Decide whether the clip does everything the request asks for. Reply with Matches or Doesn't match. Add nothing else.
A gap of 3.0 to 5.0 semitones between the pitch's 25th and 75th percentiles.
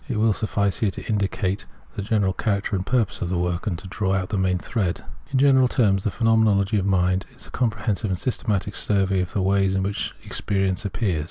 Doesn't match